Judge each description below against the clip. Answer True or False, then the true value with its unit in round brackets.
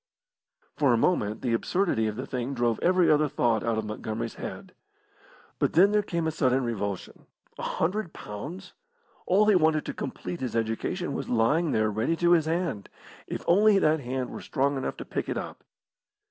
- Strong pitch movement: True (7.1 semitones)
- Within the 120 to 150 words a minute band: False (190 wpm)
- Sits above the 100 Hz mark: True (140 Hz)